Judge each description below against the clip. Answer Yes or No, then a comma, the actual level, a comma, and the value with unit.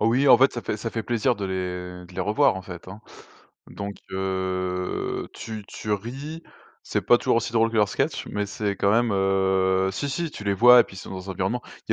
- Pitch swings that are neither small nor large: Yes, average, 3.6 semitones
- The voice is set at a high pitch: No, low, 100 Hz